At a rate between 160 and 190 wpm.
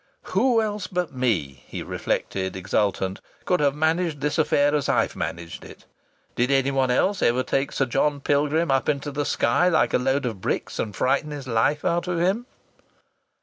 Yes: average, 180 wpm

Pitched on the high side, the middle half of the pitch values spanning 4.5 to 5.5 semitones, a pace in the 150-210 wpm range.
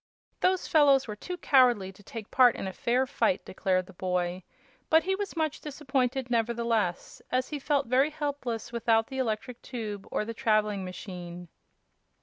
Yes: high, 235 Hz; average, 5.0 semitones; average, 165 wpm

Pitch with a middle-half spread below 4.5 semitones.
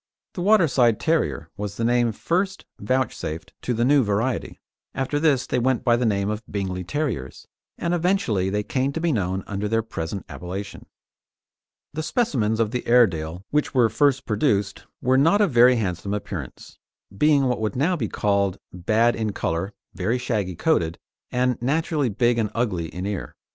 No: average, 5.1 semitones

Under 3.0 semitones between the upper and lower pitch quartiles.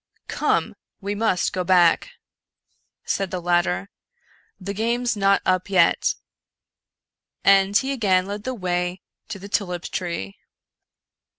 Yes: narrow, 2.4 semitones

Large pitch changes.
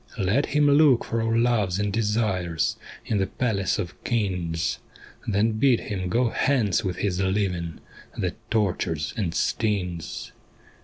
No: average, 4.0 semitones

